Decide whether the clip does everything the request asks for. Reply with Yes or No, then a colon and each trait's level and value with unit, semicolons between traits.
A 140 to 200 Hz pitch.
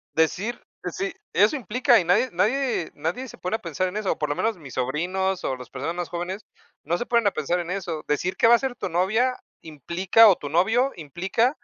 Yes: medium, 185 Hz